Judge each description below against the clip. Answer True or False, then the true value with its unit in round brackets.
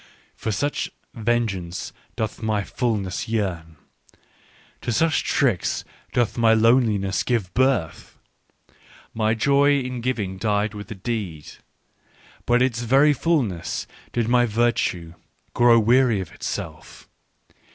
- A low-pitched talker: True (115 Hz)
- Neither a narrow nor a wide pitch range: True (3.6 semitones)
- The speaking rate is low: True (120 wpm)